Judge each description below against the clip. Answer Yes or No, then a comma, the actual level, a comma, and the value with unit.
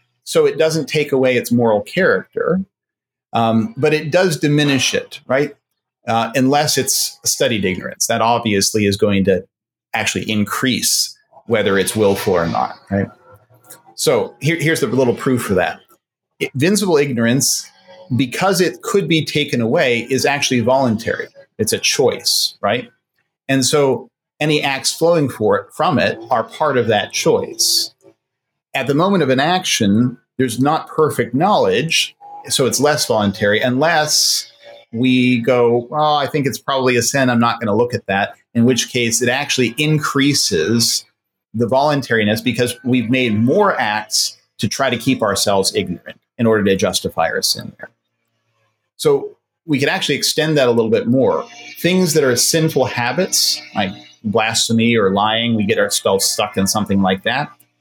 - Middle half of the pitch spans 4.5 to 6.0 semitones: Yes, average, 5.1 semitones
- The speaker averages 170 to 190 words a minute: No, average, 160 wpm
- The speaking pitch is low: Yes, low, 130 Hz